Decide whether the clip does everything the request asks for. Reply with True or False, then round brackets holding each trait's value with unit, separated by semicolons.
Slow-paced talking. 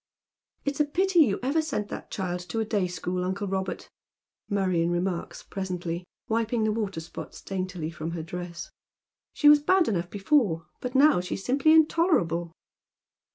False (165 wpm)